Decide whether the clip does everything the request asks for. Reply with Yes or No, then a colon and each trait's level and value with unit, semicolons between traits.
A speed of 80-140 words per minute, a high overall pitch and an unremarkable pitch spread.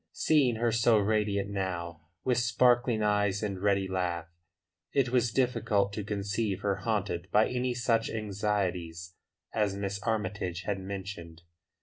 No: slow, 135 wpm; low, 100 Hz; average, 3.0 semitones